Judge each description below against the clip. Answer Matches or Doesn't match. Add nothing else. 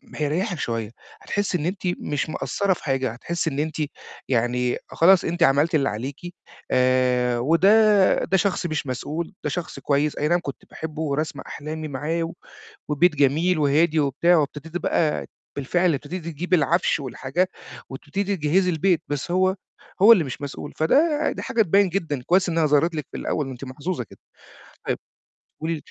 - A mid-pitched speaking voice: Matches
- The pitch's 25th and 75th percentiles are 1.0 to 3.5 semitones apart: Doesn't match